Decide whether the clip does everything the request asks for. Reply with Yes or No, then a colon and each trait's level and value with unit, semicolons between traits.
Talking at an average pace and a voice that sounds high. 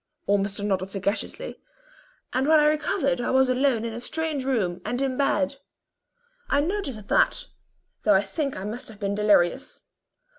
Yes: average, 165 wpm; high, 245 Hz